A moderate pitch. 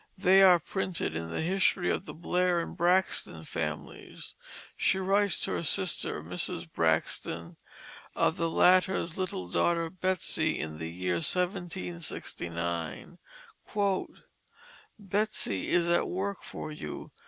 Yes: medium, 175 Hz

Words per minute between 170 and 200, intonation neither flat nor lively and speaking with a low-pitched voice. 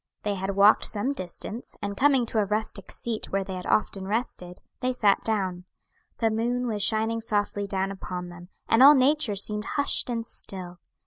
No: average, 185 wpm; average, 3.2 semitones; high, 210 Hz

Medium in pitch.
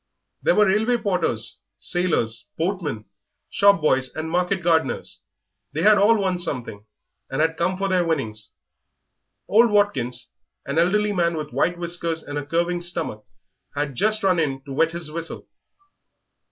Yes: medium, 170 Hz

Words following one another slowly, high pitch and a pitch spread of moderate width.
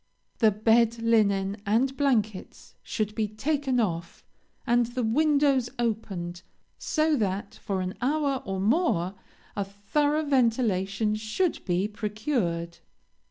Yes: slow, 115 wpm; high, 220 Hz; average, 4.8 semitones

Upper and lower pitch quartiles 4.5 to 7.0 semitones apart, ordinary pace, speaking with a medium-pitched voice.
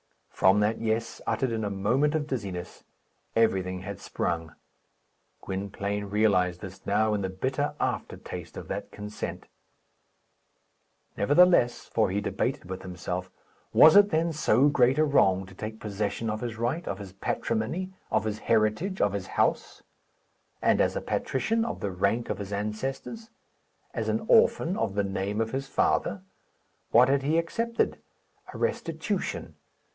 No: wide, 5.6 semitones; average, 150 wpm; low, 110 Hz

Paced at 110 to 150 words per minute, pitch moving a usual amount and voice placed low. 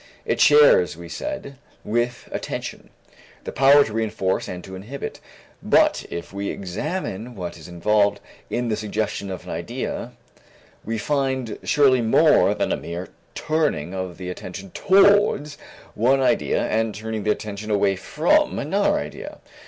No: average, 145 wpm; wide, 5.9 semitones; low, 110 Hz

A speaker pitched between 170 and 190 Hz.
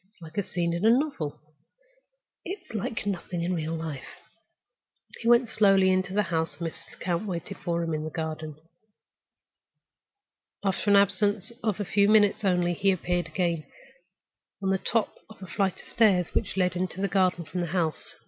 Yes: medium, 185 Hz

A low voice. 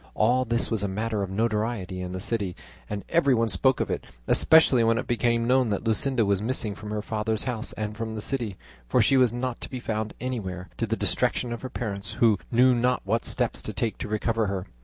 Yes: low, 115 Hz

